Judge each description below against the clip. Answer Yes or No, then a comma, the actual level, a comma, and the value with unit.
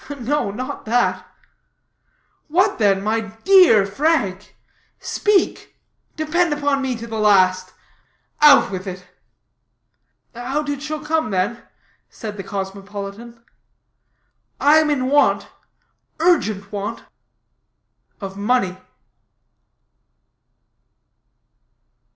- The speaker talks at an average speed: No, slow, 90 wpm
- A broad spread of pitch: Yes, wide, 6.9 semitones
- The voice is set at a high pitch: Yes, high, 230 Hz